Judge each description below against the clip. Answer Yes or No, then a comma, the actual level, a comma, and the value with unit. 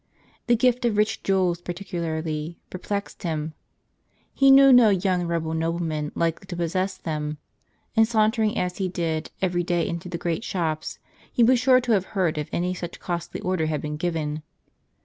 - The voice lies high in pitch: No, medium, 175 Hz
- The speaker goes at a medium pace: Yes, average, 175 wpm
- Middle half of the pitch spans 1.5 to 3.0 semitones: No, average, 3.9 semitones